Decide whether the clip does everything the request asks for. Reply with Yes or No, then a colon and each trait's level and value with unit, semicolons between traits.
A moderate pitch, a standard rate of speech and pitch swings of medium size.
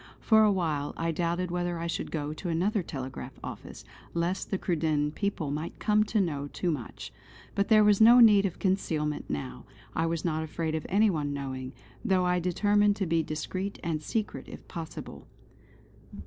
Yes: medium, 170 Hz; average, 180 wpm; average, 4.4 semitones